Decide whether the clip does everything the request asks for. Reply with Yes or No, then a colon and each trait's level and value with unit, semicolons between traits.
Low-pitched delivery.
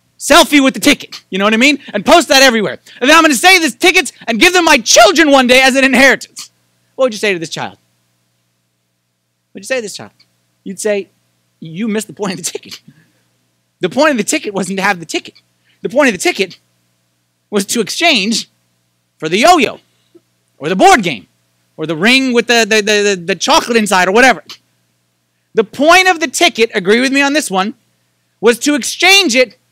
No: high, 210 Hz